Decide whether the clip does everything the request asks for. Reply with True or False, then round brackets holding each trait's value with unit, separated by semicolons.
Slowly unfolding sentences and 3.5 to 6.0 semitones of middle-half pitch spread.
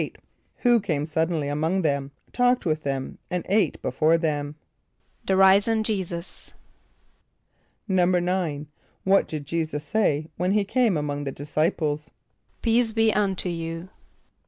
True (130 wpm; 4.7 semitones)